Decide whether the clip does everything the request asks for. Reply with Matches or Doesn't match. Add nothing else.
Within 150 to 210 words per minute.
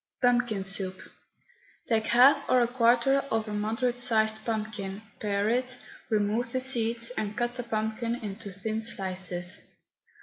Doesn't match